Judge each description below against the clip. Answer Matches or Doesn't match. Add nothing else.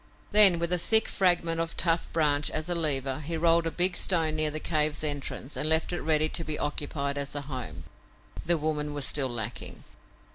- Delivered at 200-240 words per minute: Matches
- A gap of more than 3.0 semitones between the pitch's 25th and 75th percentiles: Doesn't match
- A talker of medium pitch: Matches